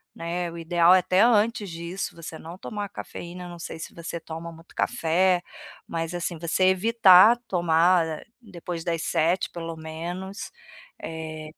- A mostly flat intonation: Yes, narrow, 2.2 semitones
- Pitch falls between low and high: Yes, medium, 170 Hz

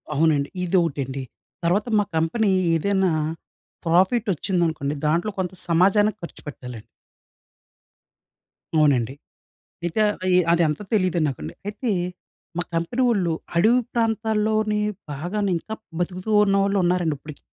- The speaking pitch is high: No, medium, 180 Hz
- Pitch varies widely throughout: No, average, 4.8 semitones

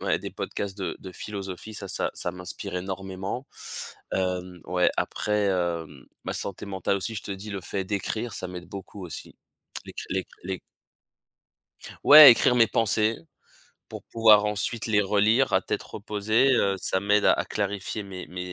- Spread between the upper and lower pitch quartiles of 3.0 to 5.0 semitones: No, narrow, 2.5 semitones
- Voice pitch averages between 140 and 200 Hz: No, low, 100 Hz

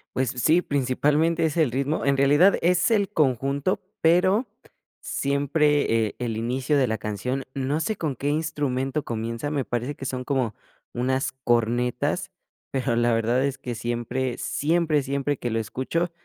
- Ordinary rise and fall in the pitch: Yes, average, 3.7 semitones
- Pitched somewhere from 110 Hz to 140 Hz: Yes, low, 135 Hz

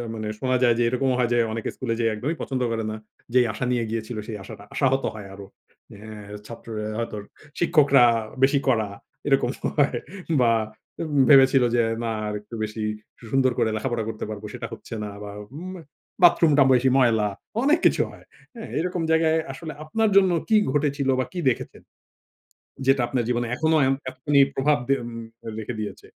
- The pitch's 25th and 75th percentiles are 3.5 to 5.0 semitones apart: Yes, average, 4.0 semitones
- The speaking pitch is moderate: No, low, 125 Hz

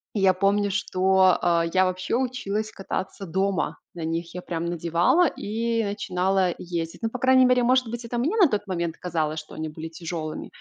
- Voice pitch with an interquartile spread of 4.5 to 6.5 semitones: Yes, average, 4.8 semitones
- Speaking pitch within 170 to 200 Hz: Yes, high, 190 Hz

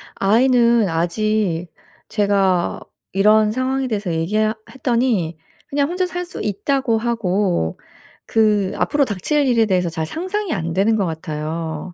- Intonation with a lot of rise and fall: Yes, wide, 5.7 semitones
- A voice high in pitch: Yes, high, 210 Hz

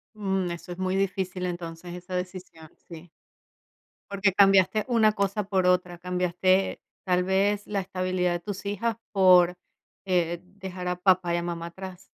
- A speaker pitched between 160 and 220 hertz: Yes, medium, 185 Hz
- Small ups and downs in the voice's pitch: Yes, narrow, 1.5 semitones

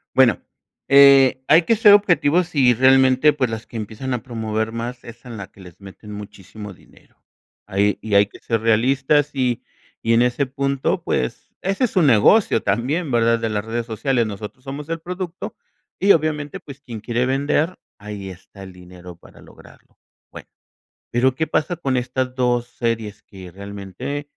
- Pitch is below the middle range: Yes, low, 125 Hz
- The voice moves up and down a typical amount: Yes, average, 4.6 semitones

